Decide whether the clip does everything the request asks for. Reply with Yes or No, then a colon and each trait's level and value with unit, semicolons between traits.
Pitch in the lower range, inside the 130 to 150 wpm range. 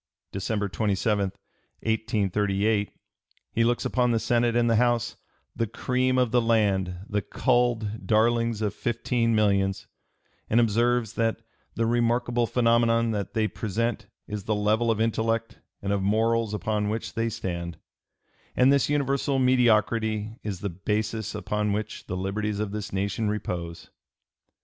Yes: low, 110 Hz; average, 140 wpm